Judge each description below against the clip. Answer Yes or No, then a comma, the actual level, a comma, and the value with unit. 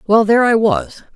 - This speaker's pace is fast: Yes, fast, 210 wpm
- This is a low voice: No, high, 210 Hz